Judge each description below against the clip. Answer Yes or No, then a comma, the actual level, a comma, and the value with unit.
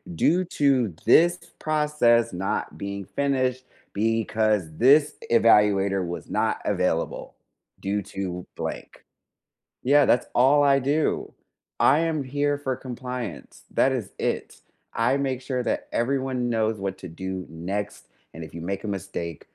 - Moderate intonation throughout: No, wide, 5.7 semitones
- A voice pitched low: Yes, low, 115 Hz